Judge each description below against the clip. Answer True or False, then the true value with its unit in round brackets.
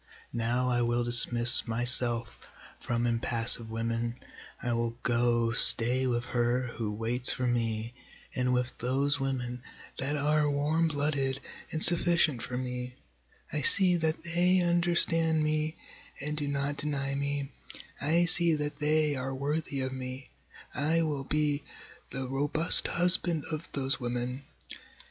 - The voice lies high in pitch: False (135 Hz)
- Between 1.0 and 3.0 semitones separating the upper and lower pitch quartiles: False (3.9 semitones)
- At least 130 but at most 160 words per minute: True (140 wpm)